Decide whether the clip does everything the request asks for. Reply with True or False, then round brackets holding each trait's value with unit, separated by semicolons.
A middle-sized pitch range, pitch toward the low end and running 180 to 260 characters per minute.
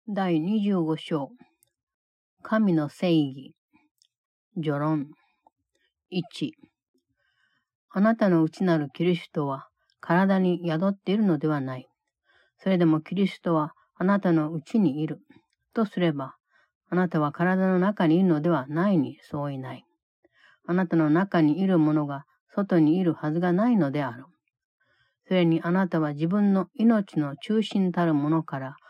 False (3.9 semitones; 170 Hz; 250 characters per minute)